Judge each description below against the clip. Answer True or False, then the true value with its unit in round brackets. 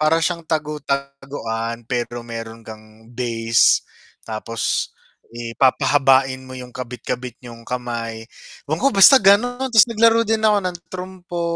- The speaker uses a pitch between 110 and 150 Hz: True (135 Hz)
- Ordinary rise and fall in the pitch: False (7.2 semitones)